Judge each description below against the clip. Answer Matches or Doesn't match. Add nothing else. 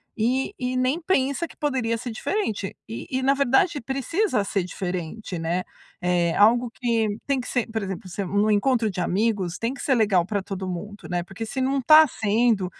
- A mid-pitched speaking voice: Doesn't match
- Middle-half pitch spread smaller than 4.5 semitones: Doesn't match